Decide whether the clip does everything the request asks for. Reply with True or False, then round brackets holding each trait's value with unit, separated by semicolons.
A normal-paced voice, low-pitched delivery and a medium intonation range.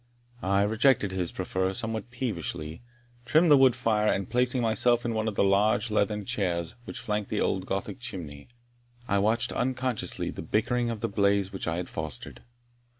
True (175 wpm; 105 Hz; 4.0 semitones)